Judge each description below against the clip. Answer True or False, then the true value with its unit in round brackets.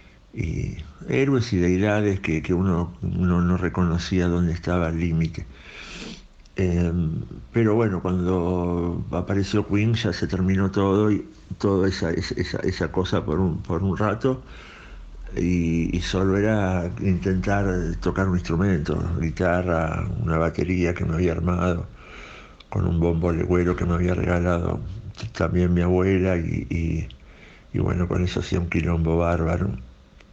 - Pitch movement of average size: False (2.0 semitones)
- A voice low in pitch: True (90 Hz)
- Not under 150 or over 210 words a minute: False (140 wpm)